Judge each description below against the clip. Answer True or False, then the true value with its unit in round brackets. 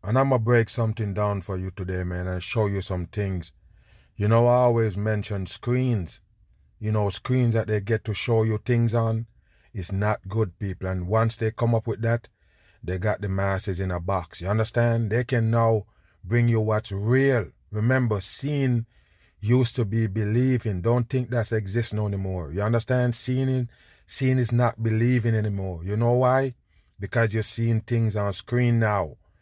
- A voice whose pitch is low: True (110 Hz)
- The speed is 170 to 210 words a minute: True (175 wpm)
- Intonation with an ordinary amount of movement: True (3.3 semitones)